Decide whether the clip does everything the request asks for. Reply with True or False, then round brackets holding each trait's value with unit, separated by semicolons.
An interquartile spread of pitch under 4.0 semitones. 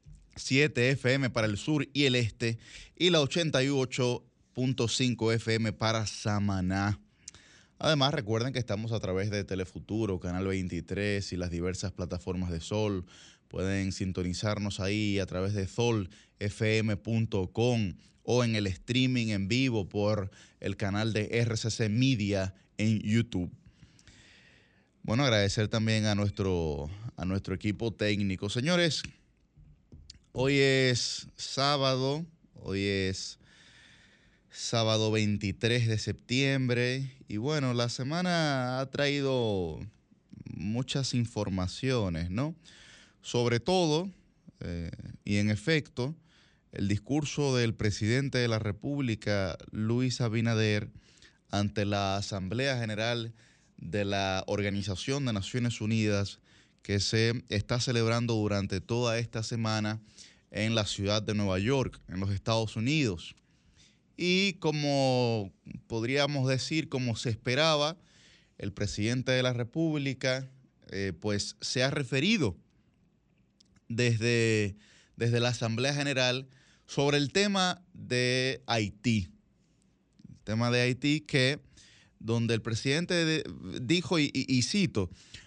False (4.3 semitones)